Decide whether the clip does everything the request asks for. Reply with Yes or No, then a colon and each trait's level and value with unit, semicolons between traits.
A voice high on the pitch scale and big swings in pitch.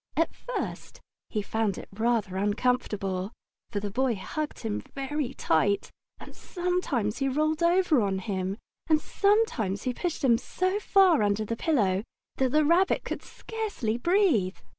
Yes: high, 245 Hz; wide, 8.2 semitones